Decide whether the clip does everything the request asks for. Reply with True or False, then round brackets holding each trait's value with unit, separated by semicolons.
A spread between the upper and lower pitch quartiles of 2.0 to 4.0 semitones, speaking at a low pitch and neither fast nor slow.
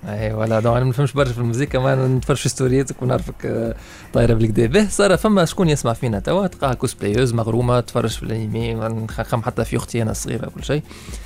False (3.4 semitones; 120 Hz; 190 wpm)